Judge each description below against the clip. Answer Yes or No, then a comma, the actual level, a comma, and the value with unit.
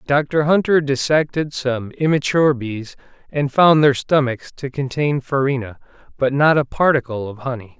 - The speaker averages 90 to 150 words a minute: Yes, average, 145 wpm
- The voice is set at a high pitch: No, low, 135 Hz